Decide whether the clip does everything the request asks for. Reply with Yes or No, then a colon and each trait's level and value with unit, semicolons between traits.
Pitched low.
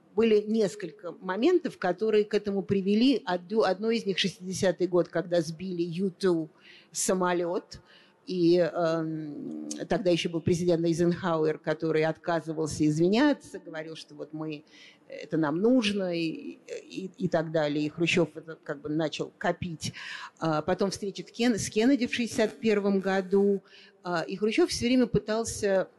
No: medium, 180 Hz